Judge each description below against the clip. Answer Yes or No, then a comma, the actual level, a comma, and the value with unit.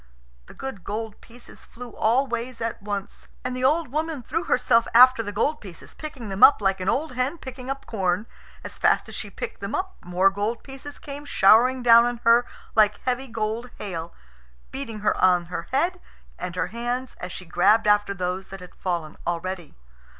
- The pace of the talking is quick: No, average, 195 wpm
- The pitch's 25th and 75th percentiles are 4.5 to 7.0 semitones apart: Yes, average, 5.0 semitones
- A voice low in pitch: No, high, 230 Hz